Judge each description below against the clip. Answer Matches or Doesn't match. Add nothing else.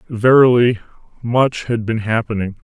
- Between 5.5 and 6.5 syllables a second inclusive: Doesn't match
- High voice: Doesn't match